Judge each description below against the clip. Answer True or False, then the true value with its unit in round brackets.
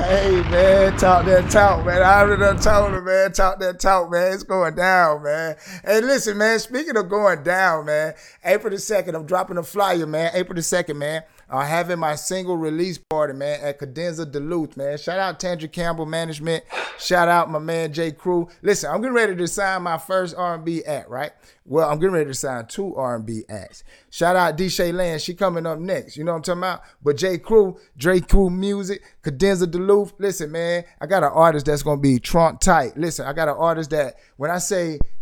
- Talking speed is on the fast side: True (215 wpm)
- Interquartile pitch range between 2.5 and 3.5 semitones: True (3.2 semitones)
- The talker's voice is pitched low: False (175 Hz)